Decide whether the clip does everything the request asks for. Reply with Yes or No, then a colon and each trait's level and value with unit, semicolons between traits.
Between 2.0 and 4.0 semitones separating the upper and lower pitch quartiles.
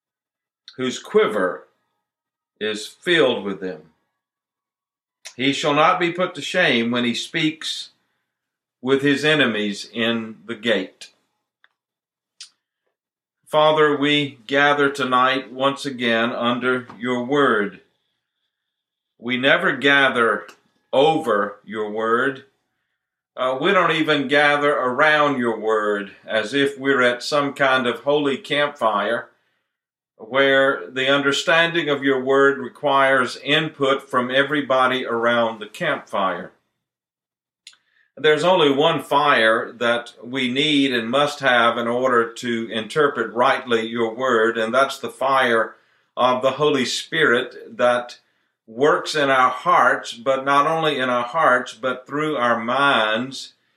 Yes: average, 3.4 semitones